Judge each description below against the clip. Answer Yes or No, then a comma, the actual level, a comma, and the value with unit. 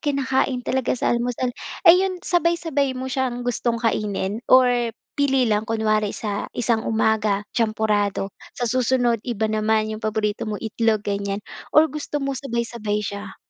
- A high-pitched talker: Yes, high, 230 Hz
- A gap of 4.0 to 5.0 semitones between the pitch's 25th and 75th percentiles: No, average, 3.4 semitones